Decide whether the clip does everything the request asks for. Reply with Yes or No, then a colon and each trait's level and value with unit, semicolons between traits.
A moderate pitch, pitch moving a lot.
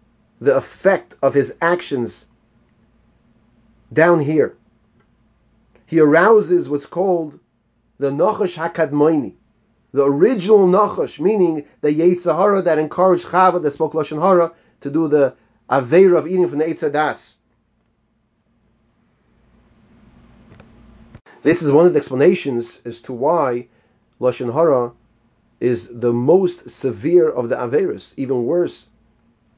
Yes: medium, 150 Hz; wide, 6.9 semitones